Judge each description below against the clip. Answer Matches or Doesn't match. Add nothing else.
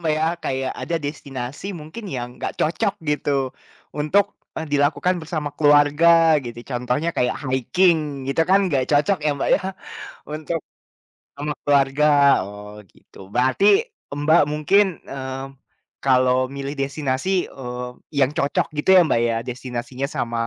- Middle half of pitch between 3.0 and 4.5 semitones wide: Matches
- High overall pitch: Doesn't match